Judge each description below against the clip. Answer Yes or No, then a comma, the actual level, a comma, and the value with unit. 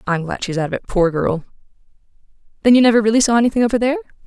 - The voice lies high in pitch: Yes, high, 215 Hz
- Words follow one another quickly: Yes, fast, 240 wpm